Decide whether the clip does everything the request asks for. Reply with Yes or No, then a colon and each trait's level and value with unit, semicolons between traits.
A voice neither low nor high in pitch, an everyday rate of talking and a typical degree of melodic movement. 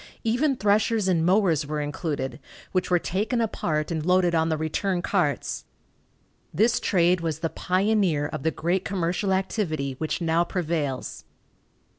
Yes: medium, 175 Hz; average, 145 wpm; average, 3.6 semitones